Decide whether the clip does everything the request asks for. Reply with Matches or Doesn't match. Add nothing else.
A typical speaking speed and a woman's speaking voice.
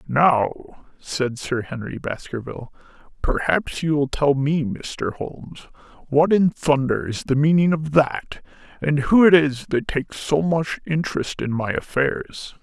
Doesn't match